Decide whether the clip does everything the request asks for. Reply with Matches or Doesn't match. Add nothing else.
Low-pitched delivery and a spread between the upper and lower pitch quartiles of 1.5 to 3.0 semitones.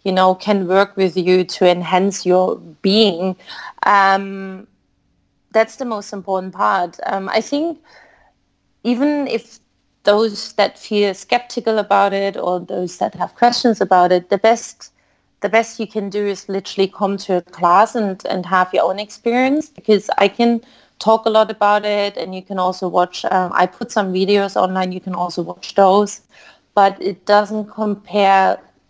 Doesn't match